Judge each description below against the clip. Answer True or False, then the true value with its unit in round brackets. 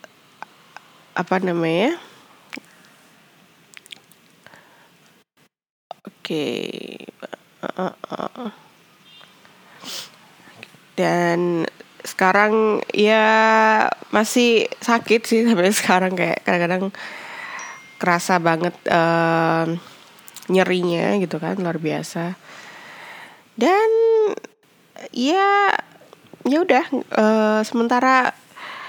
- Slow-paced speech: True (65 wpm)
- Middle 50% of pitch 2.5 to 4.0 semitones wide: False (5.1 semitones)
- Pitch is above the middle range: True (195 Hz)